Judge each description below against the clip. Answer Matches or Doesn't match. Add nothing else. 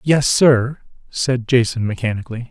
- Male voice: Matches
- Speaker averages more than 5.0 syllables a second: Doesn't match